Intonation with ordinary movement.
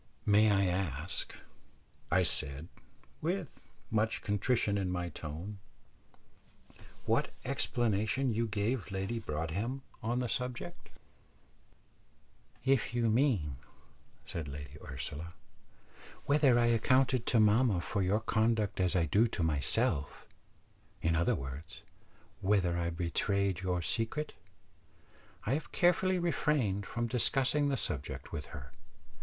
No: wide, 6.0 semitones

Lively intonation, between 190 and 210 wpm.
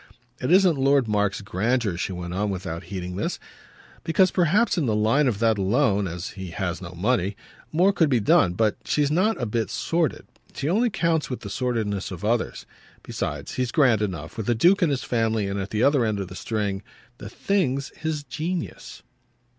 Yes: wide, 7.1 semitones; average, 195 wpm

